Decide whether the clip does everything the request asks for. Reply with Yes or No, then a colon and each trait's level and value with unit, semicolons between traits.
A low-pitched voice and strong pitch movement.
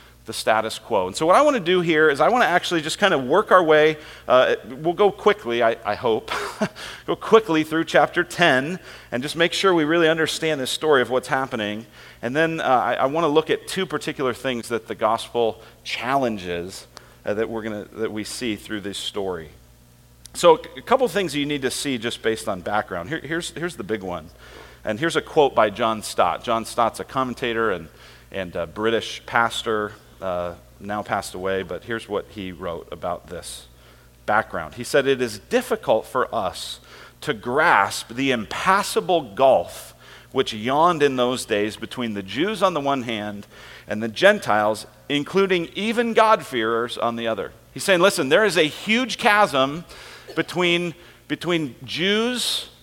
Yes: low, 125 Hz; wide, 7.3 semitones